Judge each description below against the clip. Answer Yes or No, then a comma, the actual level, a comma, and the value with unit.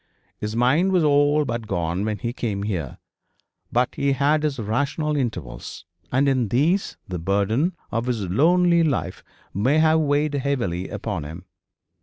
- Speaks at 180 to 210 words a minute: No, average, 155 wpm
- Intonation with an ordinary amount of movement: No, wide, 6.5 semitones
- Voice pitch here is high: No, low, 125 Hz